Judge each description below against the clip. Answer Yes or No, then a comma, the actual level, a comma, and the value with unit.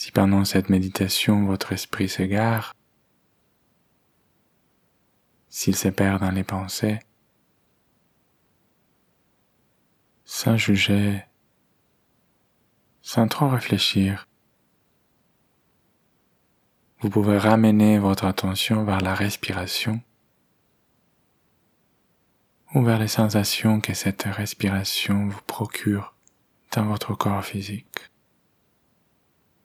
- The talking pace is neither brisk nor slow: No, slow, 80 wpm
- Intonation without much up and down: Yes, narrow, 1.9 semitones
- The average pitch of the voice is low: Yes, low, 100 Hz